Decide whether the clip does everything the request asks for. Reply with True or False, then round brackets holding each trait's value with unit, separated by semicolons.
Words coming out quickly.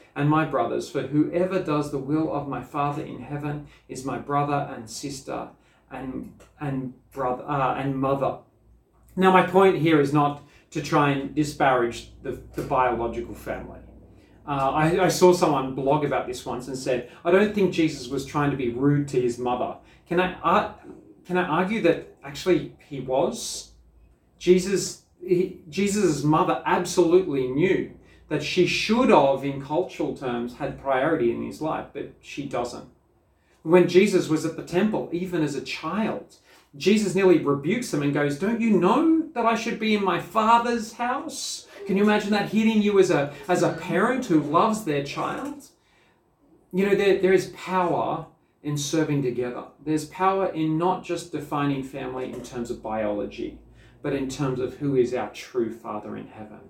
False (175 wpm)